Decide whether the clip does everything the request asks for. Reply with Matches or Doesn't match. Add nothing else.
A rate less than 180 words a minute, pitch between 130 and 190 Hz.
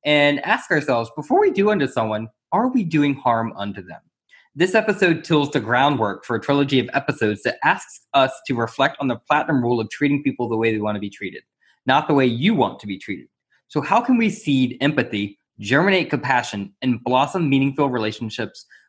Doesn't match